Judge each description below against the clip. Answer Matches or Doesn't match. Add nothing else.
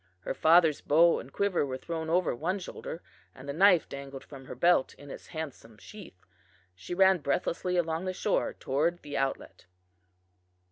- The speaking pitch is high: Doesn't match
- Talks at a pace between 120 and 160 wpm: Doesn't match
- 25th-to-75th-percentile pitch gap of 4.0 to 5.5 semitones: Matches